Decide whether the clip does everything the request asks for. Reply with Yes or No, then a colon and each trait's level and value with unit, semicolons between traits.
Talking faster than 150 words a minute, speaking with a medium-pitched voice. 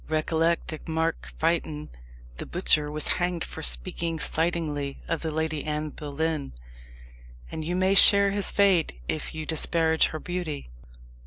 No: average, 145 wpm; medium, 160 Hz